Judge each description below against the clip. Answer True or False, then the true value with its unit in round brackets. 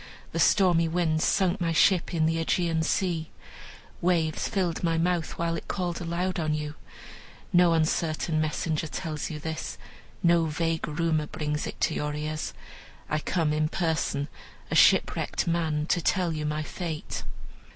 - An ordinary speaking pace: True (155 wpm)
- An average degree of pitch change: False (1.8 semitones)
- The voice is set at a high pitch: False (165 Hz)